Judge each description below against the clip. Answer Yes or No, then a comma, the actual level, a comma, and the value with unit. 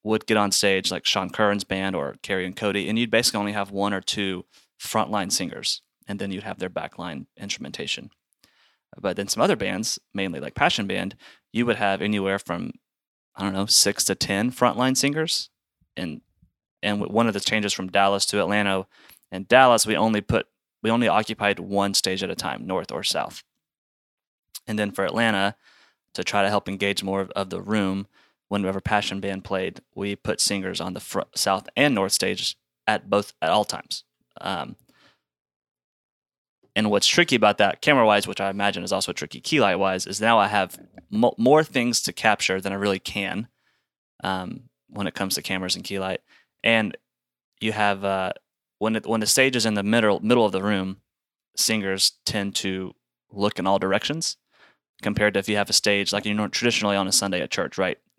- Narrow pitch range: Yes, narrow, 1.9 semitones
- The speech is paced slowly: No, average, 195 wpm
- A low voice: Yes, low, 100 Hz